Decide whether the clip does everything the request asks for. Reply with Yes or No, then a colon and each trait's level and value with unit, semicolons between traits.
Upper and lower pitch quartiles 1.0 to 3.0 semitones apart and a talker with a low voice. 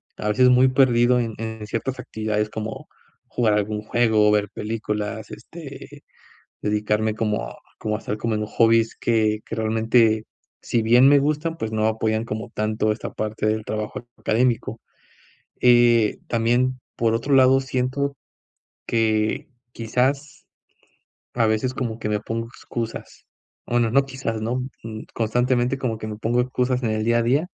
Yes: narrow, 2.4 semitones; low, 115 Hz